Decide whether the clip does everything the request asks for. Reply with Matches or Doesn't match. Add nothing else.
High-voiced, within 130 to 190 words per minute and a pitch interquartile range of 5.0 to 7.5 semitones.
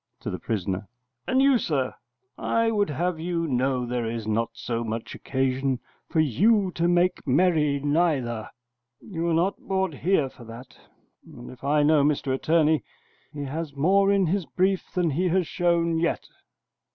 Doesn't match